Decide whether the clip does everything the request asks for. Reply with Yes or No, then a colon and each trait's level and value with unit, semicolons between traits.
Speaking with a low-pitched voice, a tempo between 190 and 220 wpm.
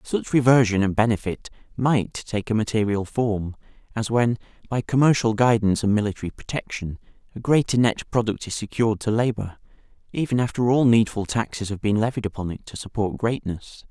No: low, 110 Hz; average, 165 wpm